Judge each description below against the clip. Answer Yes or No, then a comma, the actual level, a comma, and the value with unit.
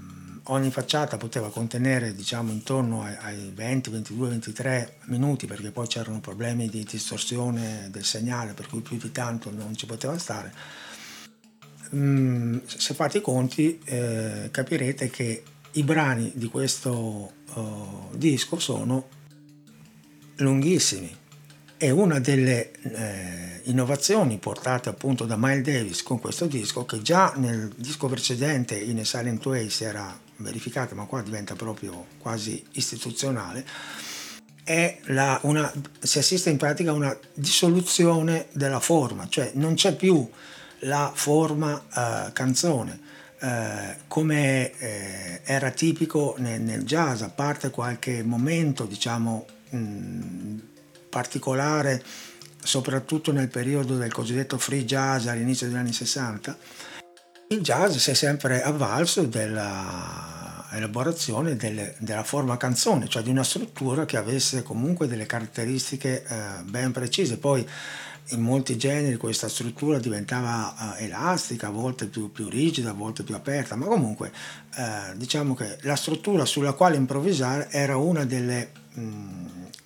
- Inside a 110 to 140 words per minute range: Yes, average, 130 wpm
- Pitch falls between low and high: No, low, 125 Hz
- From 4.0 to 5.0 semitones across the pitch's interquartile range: Yes, average, 4.3 semitones